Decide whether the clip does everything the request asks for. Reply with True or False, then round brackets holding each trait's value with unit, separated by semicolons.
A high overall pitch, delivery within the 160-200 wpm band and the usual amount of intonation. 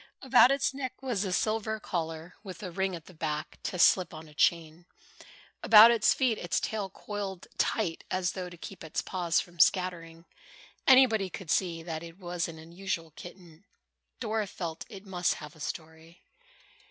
False (180 Hz; 180 wpm; 3.8 semitones)